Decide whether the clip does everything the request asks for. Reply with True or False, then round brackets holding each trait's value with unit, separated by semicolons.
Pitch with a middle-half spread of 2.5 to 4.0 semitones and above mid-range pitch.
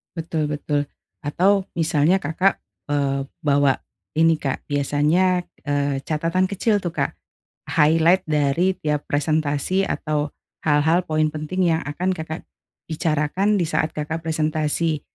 False (2.9 semitones; 155 Hz)